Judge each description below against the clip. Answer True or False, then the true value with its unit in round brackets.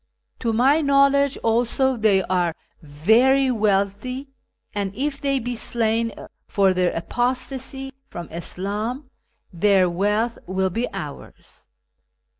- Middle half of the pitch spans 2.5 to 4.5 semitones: False (5.5 semitones)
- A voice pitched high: True (225 Hz)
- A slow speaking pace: True (110 wpm)